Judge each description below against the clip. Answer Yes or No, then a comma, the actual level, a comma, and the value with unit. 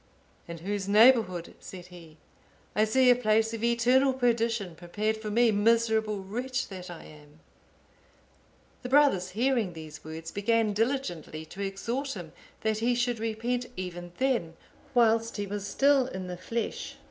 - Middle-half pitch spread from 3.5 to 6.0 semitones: Yes, average, 4.7 semitones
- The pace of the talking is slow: No, average, 150 wpm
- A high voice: Yes, high, 220 Hz